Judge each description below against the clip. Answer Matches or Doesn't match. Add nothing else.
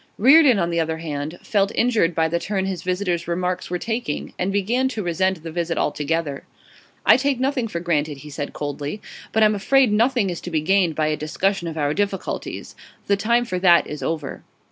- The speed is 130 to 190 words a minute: Doesn't match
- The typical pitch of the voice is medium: Matches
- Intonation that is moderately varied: Matches